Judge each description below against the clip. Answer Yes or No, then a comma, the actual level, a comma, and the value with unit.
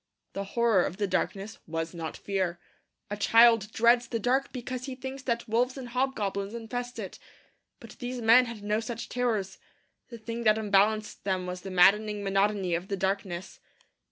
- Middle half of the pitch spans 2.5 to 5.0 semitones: Yes, average, 3.5 semitones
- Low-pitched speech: No, high, 215 Hz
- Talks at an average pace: Yes, average, 175 wpm